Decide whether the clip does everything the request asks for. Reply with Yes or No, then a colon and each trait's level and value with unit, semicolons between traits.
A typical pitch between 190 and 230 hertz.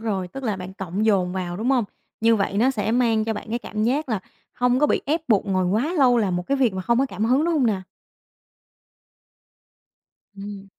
Yes: high, 220 Hz